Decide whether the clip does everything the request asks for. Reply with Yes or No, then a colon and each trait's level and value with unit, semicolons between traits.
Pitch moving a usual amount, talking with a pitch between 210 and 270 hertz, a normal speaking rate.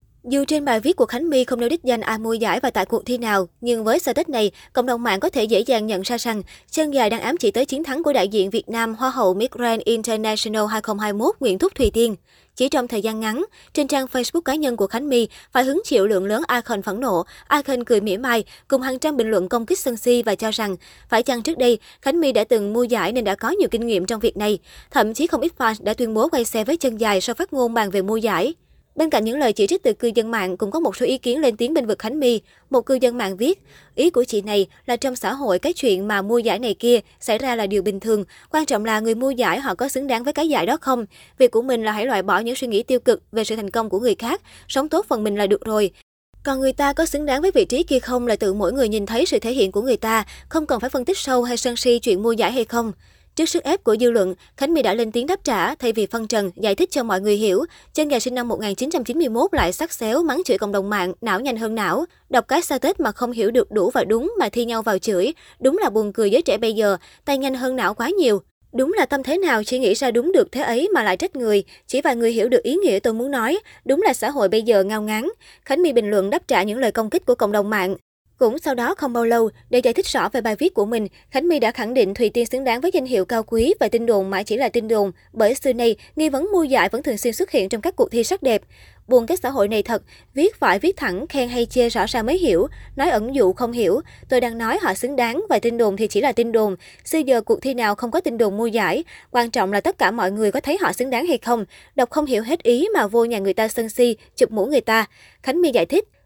No: average, 4.2 semitones; high, 240 Hz; fast, 290 wpm